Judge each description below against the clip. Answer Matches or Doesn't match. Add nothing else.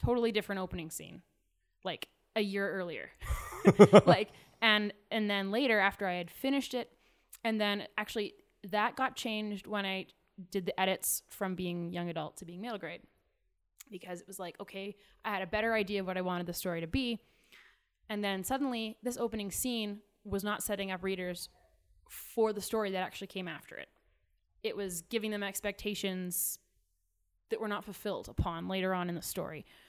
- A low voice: Doesn't match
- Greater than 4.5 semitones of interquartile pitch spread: Doesn't match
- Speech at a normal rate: Matches